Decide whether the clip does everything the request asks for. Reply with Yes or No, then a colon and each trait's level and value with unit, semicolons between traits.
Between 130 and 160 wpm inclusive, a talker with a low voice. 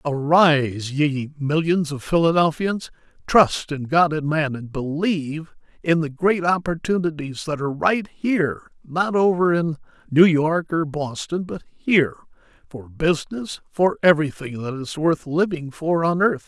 No: average, 140 wpm; medium, 160 Hz